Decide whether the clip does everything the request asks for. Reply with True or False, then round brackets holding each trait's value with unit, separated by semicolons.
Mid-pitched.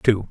False (105 Hz)